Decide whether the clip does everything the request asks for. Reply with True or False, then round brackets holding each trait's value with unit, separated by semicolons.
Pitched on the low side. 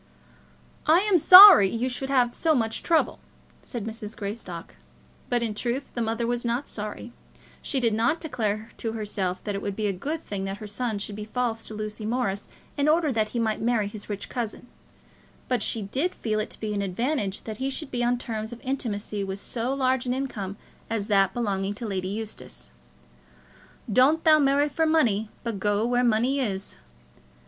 False (225 Hz)